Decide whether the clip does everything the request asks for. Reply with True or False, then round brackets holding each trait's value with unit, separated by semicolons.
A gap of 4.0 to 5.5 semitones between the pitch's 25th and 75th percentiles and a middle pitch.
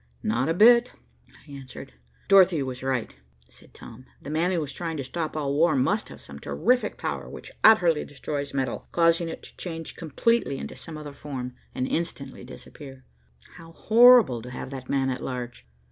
True (4.5 semitones; 145 Hz)